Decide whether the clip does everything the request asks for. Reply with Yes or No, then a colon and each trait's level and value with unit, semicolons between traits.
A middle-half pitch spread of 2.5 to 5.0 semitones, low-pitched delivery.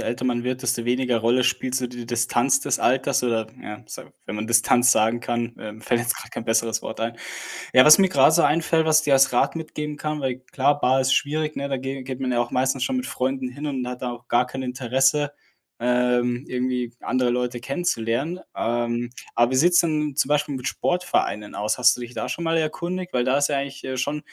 Yes: average, 2.9 semitones; low, 130 Hz